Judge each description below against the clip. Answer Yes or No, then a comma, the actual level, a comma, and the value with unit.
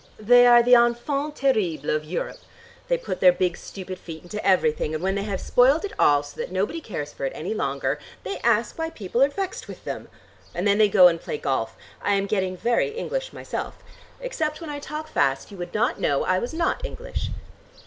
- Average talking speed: No, fast, 215 wpm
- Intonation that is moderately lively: No, wide, 8.0 semitones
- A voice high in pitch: Yes, high, 205 Hz